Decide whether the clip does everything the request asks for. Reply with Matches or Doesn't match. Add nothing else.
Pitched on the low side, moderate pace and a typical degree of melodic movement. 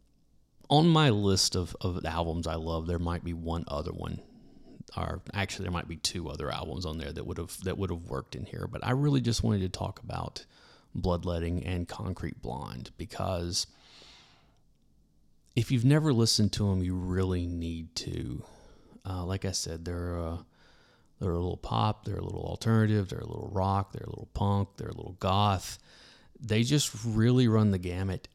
Matches